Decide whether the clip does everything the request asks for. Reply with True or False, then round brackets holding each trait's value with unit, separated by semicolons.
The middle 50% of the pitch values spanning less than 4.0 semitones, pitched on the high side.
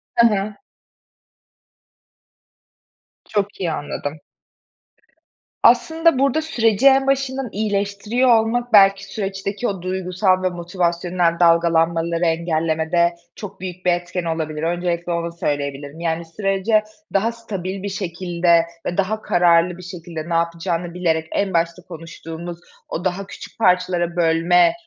False (3.0 semitones; 180 Hz)